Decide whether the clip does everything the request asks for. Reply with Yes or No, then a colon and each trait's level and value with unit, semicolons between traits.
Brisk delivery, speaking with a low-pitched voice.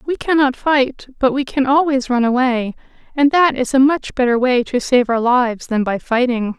No: fast, 210 wpm; very high, 255 Hz